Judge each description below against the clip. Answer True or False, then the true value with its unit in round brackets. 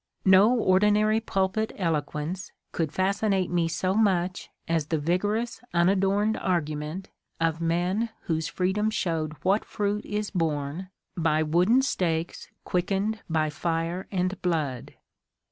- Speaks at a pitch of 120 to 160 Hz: False (180 Hz)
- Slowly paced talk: True (125 wpm)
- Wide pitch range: False (3.6 semitones)